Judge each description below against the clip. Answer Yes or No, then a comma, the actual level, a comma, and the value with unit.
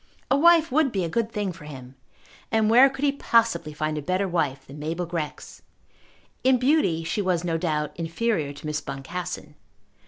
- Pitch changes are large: Yes, wide, 7.3 semitones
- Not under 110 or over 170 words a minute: No, average, 185 wpm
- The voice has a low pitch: No, medium, 175 Hz